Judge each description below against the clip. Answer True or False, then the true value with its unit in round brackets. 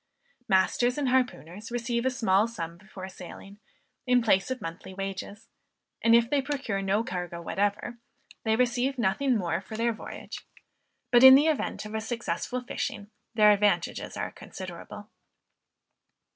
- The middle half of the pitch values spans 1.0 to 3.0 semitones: False (4.1 semitones)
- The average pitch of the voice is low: False (220 Hz)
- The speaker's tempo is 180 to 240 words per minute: False (145 wpm)